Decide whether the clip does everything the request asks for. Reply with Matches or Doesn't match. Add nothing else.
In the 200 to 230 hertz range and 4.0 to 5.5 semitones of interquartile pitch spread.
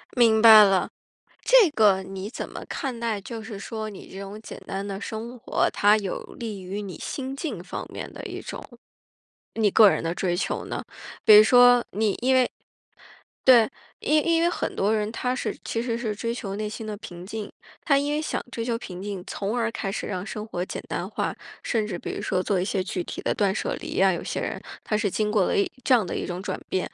Doesn't match